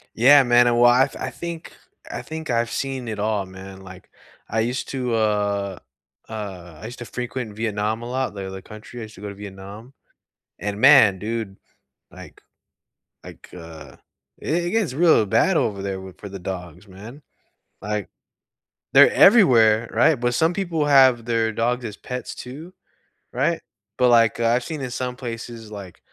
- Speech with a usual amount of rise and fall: Yes, average, 4.0 semitones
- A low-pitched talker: Yes, low, 115 Hz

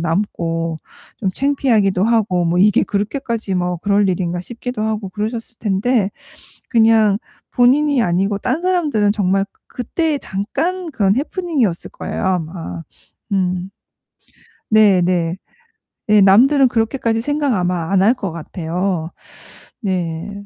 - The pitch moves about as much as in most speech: Yes, average, 4.8 semitones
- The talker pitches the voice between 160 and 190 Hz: No, high, 205 Hz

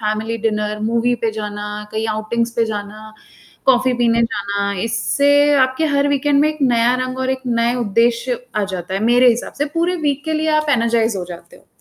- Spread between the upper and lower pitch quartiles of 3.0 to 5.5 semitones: Yes, average, 3.4 semitones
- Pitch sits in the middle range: No, high, 230 Hz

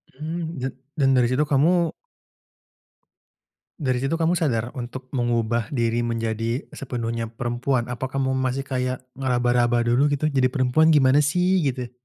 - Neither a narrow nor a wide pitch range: Yes, average, 3.1 semitones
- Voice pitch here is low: Yes, low, 130 Hz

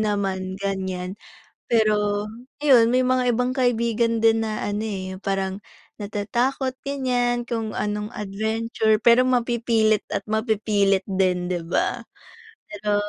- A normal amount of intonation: Yes, average, 3.1 semitones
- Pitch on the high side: Yes, high, 215 Hz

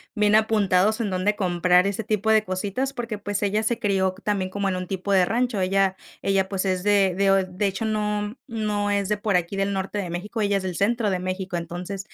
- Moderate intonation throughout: No, narrow, 2.1 semitones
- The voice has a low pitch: No, high, 200 Hz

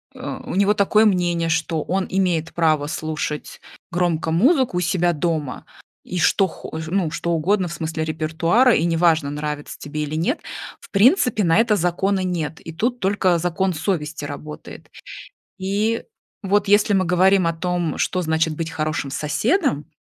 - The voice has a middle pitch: Yes, medium, 175 Hz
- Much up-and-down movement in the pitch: No, average, 3.5 semitones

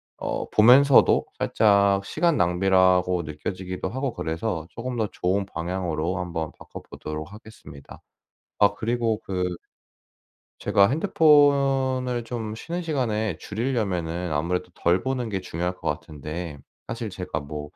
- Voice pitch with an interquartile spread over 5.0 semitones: Yes, wide, 5.5 semitones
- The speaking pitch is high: No, low, 100 Hz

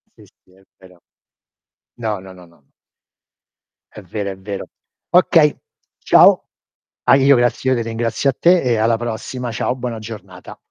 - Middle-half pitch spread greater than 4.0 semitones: Yes, average, 4.6 semitones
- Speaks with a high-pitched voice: No, low, 115 Hz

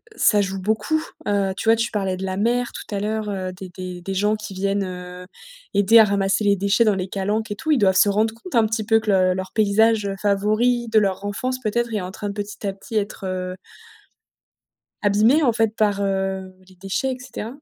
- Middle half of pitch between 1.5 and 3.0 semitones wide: Yes, narrow, 2.4 semitones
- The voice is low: No, high, 205 Hz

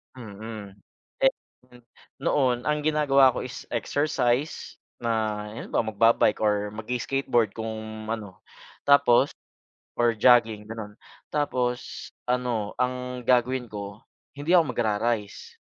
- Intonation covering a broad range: No, average, 2.8 semitones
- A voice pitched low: Yes, low, 120 Hz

